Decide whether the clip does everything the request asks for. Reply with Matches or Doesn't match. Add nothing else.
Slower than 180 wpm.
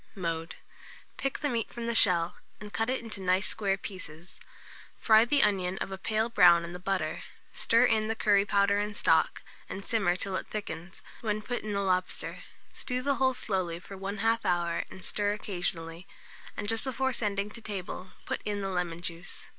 Doesn't match